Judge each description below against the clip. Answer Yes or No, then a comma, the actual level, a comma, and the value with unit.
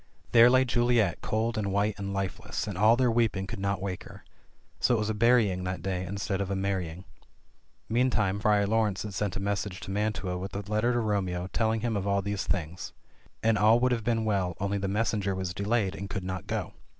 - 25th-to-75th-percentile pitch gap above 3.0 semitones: No, narrow, 2.6 semitones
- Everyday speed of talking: No, fast, 225 wpm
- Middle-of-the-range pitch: No, low, 100 Hz